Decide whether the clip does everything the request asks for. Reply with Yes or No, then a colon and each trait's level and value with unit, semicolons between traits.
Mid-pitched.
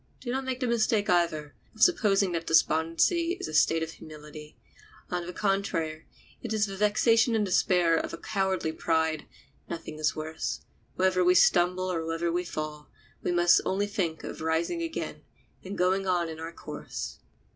Yes: medium, 175 Hz